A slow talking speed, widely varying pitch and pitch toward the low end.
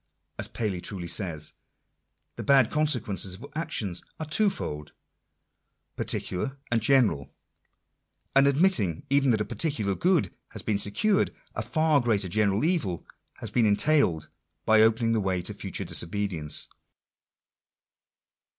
Yes: slow, 125 wpm; wide, 6.8 semitones; low, 110 Hz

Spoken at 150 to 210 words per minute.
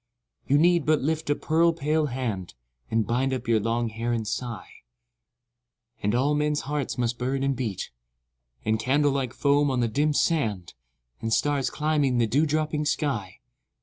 Yes: average, 170 wpm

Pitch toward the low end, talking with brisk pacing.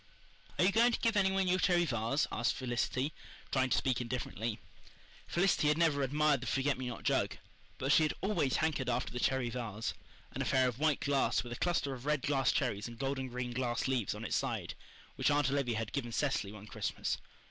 Yes: low, 130 Hz; fast, 215 wpm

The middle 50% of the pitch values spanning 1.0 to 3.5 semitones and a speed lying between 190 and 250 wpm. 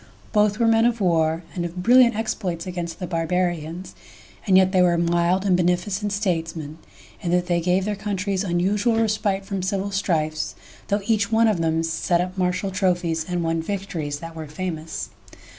No: average, 3.2 semitones; average, 180 wpm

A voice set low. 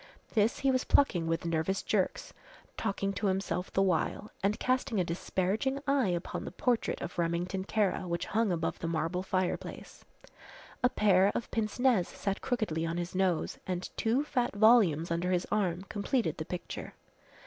No: high, 190 Hz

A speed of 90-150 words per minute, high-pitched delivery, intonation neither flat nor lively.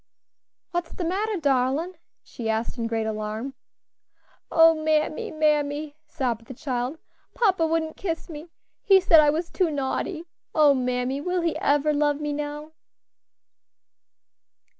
Yes: slow, 135 wpm; very high, 300 Hz; average, 3.8 semitones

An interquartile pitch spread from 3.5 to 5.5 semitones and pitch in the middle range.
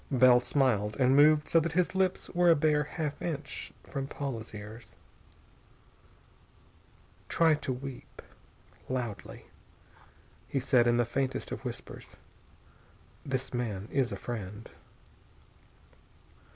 No: average, 3.9 semitones; low, 130 Hz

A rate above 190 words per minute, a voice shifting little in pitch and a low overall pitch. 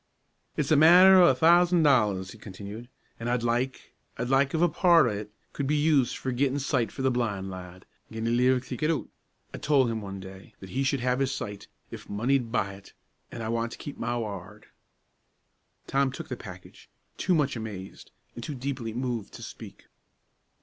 No: fast, 205 wpm; average, 4.6 semitones; low, 125 Hz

